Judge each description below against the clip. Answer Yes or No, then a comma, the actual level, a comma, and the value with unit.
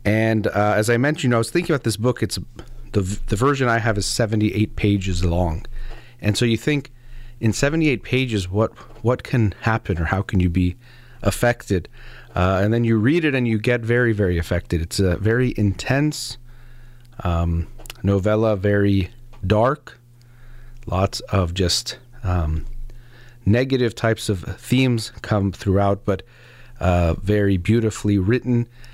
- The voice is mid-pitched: No, low, 115 Hz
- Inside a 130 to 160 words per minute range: Yes, average, 155 wpm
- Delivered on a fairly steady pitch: No, average, 3.6 semitones